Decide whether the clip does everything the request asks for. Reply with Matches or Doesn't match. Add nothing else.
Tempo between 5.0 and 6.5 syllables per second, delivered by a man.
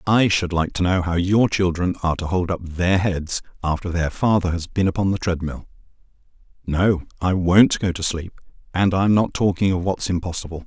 Matches